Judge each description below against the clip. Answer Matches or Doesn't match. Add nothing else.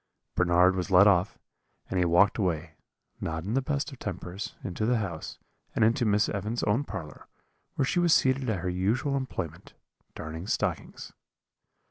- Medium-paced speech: Matches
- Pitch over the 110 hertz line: Doesn't match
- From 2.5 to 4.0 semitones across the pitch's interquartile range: Doesn't match